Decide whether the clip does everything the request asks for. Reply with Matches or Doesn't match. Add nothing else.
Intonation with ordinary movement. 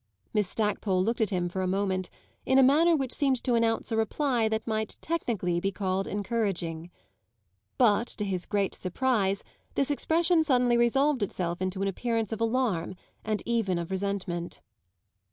Matches